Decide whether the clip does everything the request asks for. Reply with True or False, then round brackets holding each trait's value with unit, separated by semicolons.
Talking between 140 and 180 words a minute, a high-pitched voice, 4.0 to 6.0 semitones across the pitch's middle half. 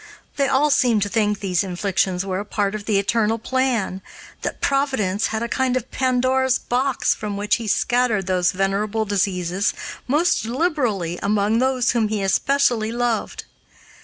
True (160 wpm; 220 Hz; 4.3 semitones)